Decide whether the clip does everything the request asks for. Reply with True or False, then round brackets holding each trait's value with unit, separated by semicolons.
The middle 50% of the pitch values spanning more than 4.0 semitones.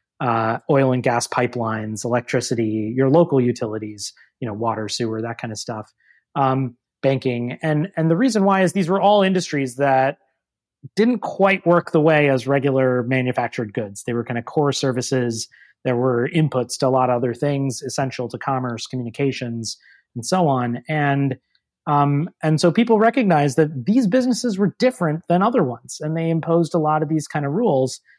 True (4.7 semitones)